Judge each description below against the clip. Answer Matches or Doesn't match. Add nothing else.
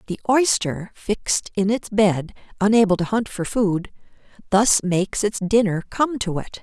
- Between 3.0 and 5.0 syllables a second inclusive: Matches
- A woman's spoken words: Matches